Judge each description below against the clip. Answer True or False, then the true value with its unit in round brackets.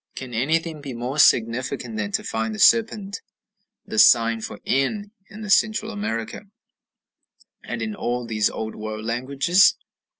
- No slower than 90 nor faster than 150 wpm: True (140 wpm)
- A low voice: True (125 Hz)